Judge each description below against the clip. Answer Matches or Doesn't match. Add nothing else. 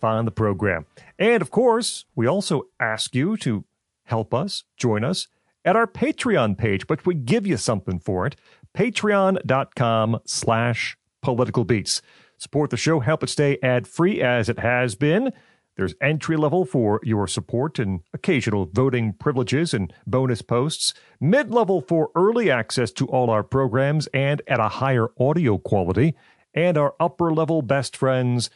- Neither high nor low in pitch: Doesn't match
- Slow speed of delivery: Doesn't match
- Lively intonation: Matches